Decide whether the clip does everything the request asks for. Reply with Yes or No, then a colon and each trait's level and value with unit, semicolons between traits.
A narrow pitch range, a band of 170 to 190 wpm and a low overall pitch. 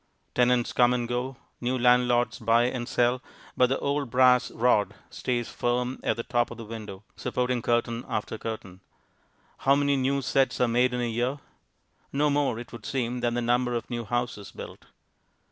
Yes: narrow, 1.2 semitones; average, 180 wpm; low, 120 Hz